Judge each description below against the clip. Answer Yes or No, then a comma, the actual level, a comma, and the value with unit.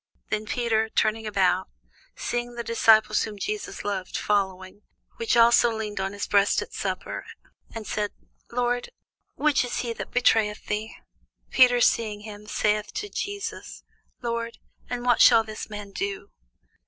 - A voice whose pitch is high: Yes, high, 220 Hz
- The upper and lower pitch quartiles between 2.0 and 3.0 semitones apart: Yes, average, 2.7 semitones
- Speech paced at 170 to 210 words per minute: No, average, 145 wpm